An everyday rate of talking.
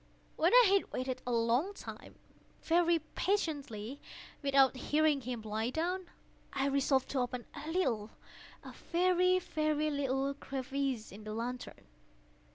No: slow, 130 wpm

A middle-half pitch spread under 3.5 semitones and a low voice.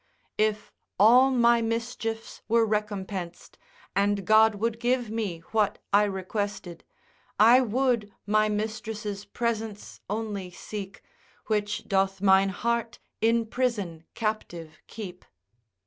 No: narrow, 2.4 semitones; high, 215 Hz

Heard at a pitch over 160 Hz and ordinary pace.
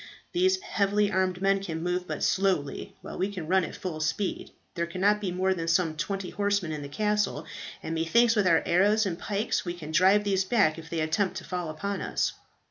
No: medium, 185 Hz; fast, 215 wpm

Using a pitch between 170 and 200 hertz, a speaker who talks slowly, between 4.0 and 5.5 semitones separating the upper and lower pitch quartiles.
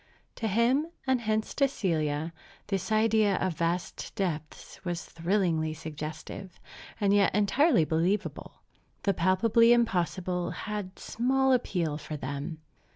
Yes: high, 190 Hz; slow, 120 wpm; average, 5.0 semitones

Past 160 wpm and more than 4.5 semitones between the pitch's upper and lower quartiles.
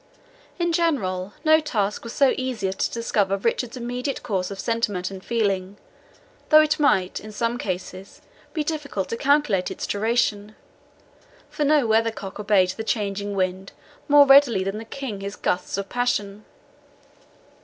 No: average, 155 wpm; average, 4.9 semitones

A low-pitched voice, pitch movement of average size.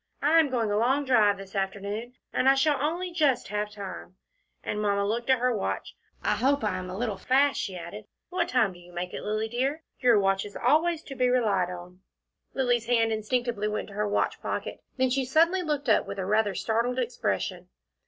No: high, 230 Hz; average, 4.6 semitones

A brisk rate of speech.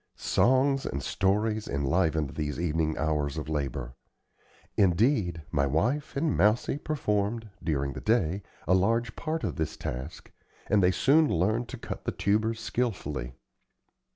No: average, 140 wpm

